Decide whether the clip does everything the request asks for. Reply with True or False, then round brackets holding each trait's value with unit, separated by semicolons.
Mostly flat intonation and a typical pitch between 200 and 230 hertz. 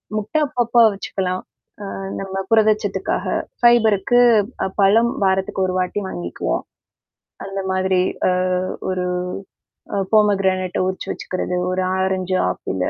False (2.3 semitones; 190 Hz)